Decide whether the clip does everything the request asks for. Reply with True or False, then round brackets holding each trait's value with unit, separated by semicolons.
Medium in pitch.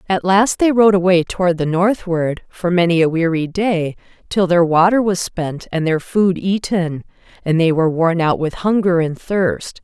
True (180 Hz)